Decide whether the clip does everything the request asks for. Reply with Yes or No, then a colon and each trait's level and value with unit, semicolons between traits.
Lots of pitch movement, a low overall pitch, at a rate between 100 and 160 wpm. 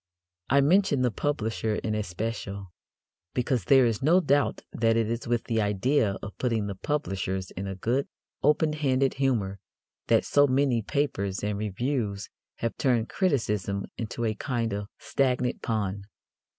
No: average, 4.9 semitones; low, 115 Hz; average, 150 wpm